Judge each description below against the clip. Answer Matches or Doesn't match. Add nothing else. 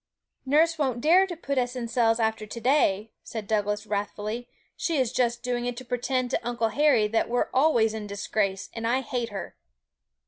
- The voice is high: Matches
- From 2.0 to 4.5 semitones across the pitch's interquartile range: Matches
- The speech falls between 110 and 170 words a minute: Doesn't match